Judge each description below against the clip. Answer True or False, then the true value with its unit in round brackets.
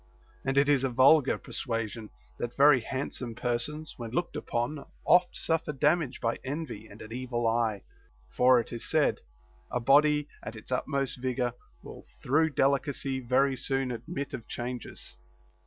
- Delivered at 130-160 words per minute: True (155 wpm)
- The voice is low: True (130 Hz)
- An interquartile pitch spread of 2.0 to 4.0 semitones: True (3.1 semitones)